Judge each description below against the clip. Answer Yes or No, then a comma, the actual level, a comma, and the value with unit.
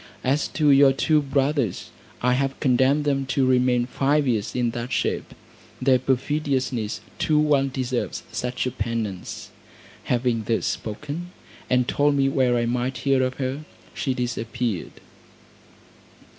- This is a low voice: Yes, low, 130 Hz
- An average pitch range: No, narrow, 2.3 semitones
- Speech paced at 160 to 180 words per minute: No, average, 140 wpm